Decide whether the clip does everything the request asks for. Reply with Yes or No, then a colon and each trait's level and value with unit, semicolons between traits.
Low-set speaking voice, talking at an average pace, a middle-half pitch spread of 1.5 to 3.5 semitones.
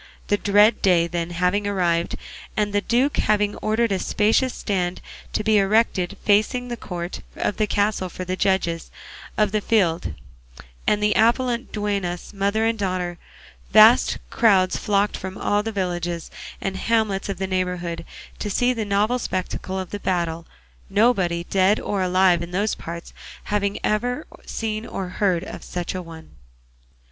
No: high, 200 Hz; average, 160 wpm; average, 2.9 semitones